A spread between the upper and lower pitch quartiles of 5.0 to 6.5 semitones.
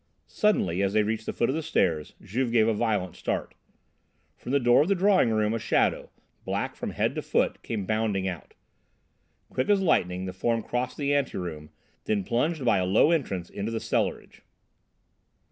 Yes: wide, 5.6 semitones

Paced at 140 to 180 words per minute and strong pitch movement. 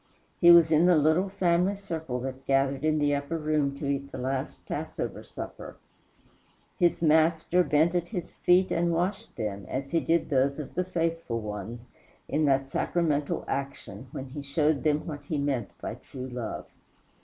No: average, 175 wpm; average, 3.8 semitones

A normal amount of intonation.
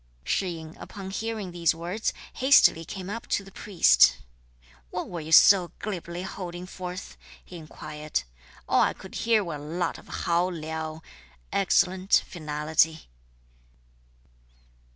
Yes: average, 3.2 semitones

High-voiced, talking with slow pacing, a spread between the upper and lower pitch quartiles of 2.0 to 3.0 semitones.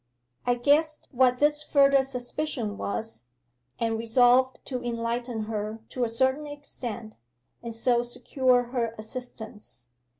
Yes: high, 245 Hz; slow, 125 wpm; narrow, 2.6 semitones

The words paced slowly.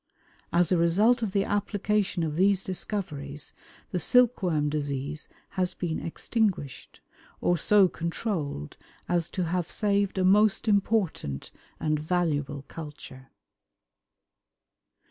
Yes: slow, 110 wpm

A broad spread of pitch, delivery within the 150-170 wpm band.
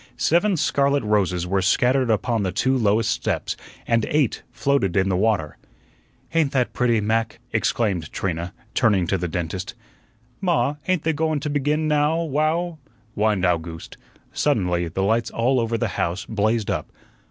Yes: wide, 6.9 semitones; average, 160 wpm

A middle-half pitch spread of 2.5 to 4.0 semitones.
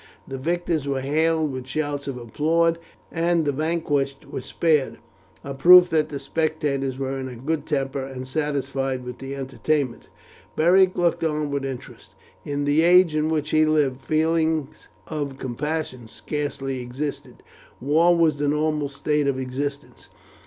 Yes: average, 2.8 semitones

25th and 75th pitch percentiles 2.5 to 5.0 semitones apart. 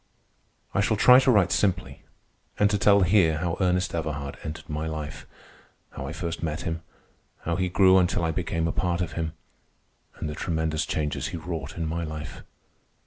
Yes: average, 2.8 semitones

